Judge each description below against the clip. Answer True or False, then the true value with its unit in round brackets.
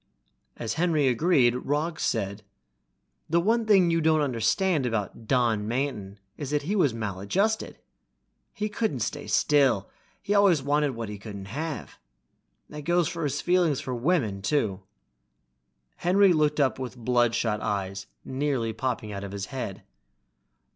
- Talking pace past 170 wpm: False (145 wpm)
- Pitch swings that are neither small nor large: False (6.6 semitones)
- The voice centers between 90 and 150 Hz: True (135 Hz)